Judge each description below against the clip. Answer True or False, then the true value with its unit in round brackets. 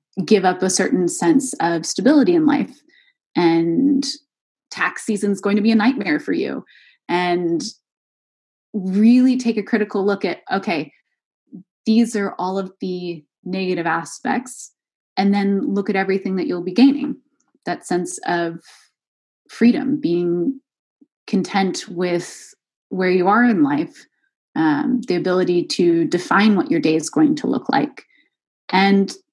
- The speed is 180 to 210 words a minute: False (145 wpm)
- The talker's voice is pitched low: False (200 Hz)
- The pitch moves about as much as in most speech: False (7.0 semitones)